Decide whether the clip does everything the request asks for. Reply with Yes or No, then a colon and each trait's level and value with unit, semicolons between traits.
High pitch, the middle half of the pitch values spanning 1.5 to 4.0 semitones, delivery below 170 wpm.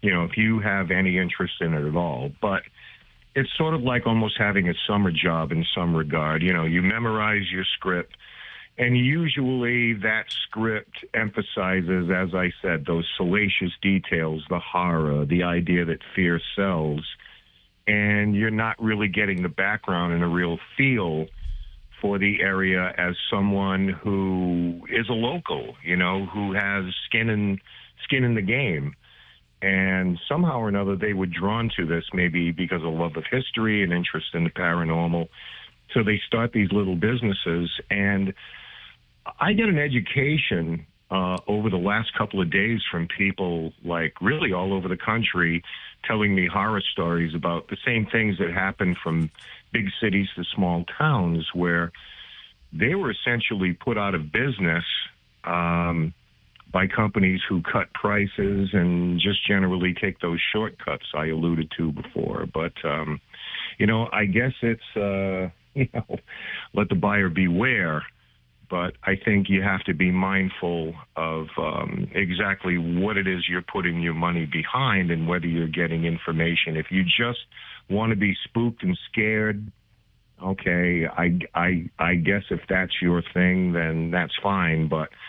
No: very low, 95 Hz; average, 3.6 semitones; average, 160 wpm